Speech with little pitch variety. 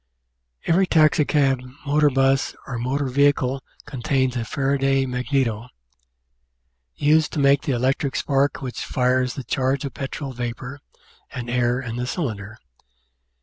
Yes: narrow, 2.1 semitones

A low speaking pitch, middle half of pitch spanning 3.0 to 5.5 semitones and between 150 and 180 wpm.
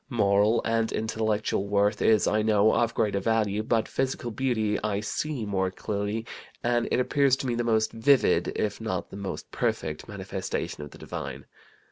No: low, 110 Hz; narrow, 2.4 semitones; average, 170 wpm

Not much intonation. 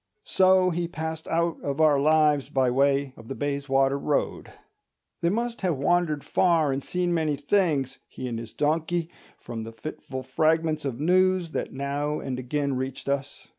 No: average, 3.6 semitones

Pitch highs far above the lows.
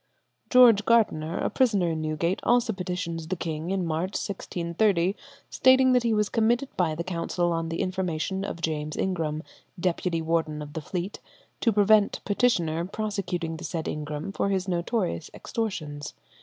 No: average, 4.0 semitones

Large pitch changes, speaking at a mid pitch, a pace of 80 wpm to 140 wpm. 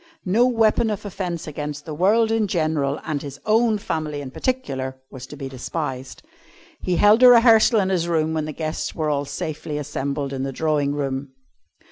No: wide, 6.5 semitones; medium, 155 Hz; average, 185 wpm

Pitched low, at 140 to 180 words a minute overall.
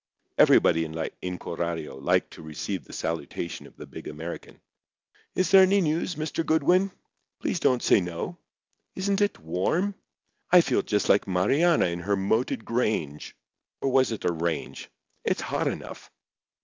Yes: low, 105 Hz; average, 145 wpm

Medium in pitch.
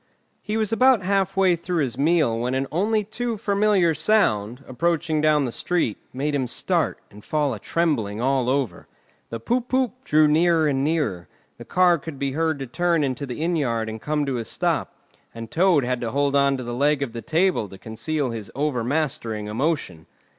Yes: medium, 145 Hz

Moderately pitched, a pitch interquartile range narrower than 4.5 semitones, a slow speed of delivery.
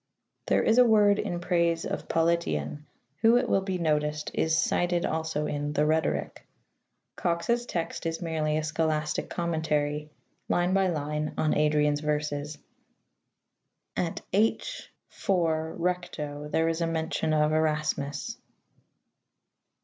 Yes: medium, 160 Hz; narrow, 2.5 semitones; slow, 125 wpm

